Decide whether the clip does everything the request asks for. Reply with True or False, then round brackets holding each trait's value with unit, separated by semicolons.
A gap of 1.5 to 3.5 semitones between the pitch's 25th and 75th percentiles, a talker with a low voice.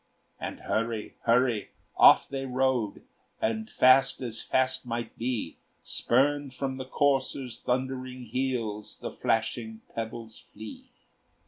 True (2.8 semitones; 125 Hz)